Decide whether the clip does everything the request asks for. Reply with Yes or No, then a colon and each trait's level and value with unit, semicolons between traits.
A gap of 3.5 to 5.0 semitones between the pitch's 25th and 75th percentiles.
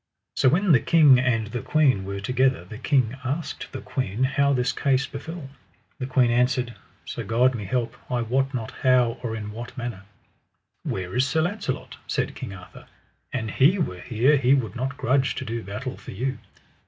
No: average, 3.0 semitones